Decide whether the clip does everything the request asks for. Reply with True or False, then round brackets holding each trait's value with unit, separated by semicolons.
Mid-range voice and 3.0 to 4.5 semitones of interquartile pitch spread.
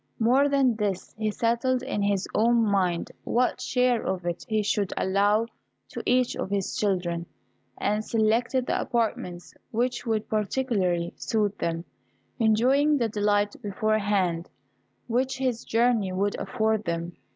False (215 Hz; 3.4 semitones)